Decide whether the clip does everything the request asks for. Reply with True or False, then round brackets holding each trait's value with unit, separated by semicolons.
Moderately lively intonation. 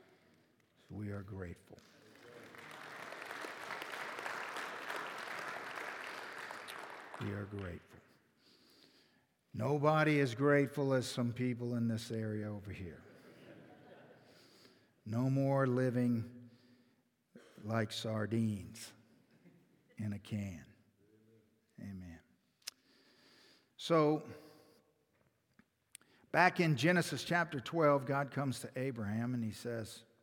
True (4.3 semitones)